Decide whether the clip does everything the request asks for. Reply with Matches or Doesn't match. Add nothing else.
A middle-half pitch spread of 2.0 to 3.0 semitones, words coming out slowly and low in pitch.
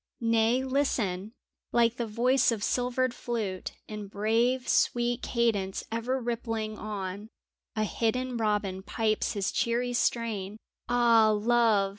Doesn't match